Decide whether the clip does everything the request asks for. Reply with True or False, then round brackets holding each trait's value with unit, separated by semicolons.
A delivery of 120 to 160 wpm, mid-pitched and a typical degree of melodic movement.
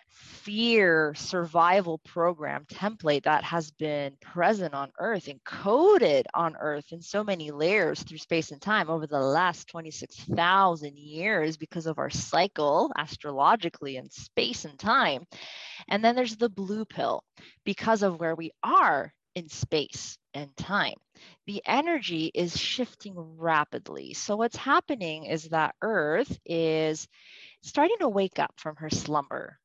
True (140 wpm; 165 Hz; 5.0 semitones)